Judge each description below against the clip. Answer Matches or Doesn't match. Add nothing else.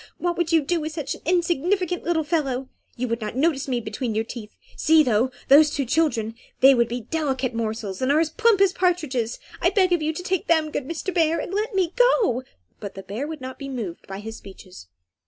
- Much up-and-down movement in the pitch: Matches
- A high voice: Matches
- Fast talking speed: Matches